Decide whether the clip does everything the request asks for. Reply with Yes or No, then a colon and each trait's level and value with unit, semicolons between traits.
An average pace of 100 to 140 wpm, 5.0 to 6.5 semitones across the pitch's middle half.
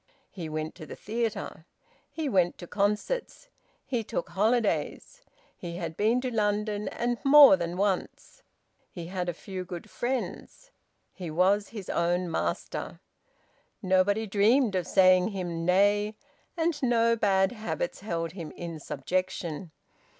No: slow, 135 wpm; average, 4.4 semitones